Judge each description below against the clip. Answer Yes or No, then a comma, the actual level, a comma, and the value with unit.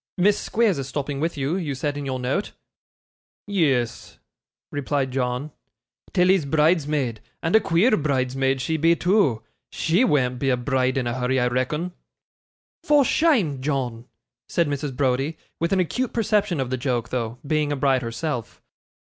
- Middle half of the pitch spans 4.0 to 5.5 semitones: Yes, average, 4.7 semitones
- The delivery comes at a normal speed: Yes, average, 160 wpm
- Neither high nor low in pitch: Yes, medium, 145 Hz